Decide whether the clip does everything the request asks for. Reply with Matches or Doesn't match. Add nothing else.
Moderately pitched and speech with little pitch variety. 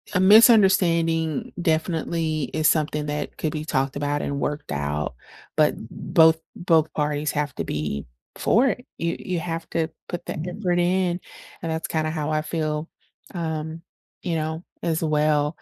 Matches